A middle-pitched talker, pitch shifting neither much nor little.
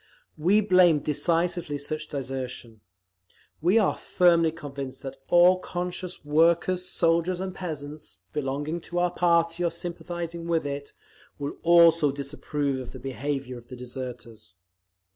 Yes: medium, 160 Hz; average, 3.8 semitones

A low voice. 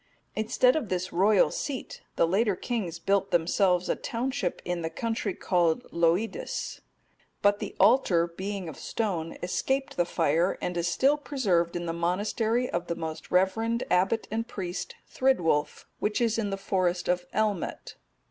No: high, 190 Hz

